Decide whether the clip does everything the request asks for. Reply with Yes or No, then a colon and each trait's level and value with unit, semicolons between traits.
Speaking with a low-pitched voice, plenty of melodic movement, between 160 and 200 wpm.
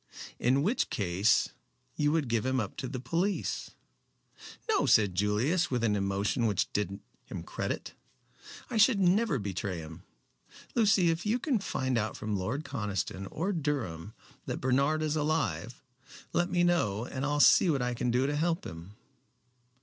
Yes: low, 130 Hz; wide, 8.0 semitones; average, 165 wpm